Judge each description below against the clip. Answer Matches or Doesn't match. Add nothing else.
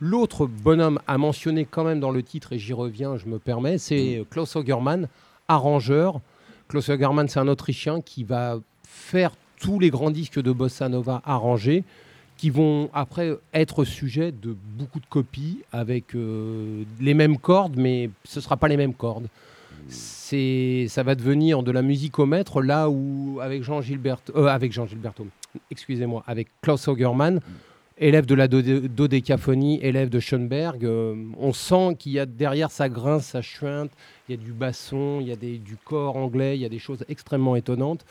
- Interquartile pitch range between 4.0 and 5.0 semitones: Doesn't match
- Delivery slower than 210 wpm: Matches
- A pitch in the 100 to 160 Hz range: Matches